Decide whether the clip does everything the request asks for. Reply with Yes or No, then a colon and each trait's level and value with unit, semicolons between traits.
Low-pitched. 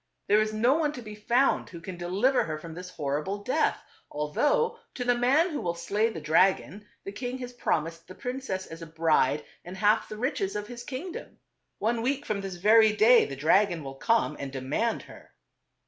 No: high, 210 Hz